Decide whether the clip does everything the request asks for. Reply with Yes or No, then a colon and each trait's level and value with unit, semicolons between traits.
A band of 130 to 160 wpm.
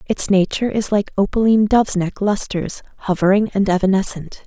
Yes: slow, 135 wpm